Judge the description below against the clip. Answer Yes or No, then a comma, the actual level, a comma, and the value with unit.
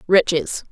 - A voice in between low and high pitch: Yes, medium, 180 Hz